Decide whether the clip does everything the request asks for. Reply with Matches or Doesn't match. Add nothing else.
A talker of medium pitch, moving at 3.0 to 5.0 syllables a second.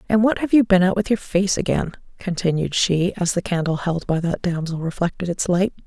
Doesn't match